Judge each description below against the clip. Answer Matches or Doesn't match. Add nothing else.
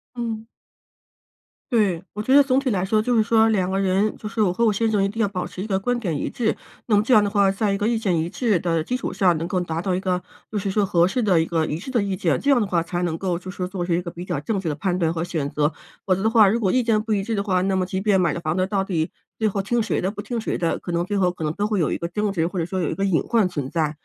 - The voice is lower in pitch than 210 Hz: Matches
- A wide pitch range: Doesn't match